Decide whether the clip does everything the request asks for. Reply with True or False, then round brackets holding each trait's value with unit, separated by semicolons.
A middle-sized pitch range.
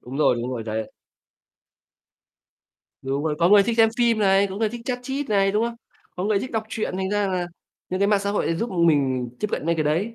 False (5.8 semitones)